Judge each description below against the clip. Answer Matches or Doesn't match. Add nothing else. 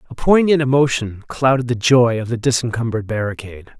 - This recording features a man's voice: Matches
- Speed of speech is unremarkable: Matches